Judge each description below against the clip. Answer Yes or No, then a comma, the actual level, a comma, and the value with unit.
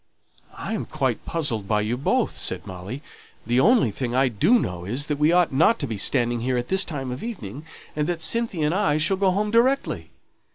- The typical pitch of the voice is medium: Yes, medium, 145 Hz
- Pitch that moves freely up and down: Yes, wide, 7.5 semitones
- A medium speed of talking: No, fast, 215 wpm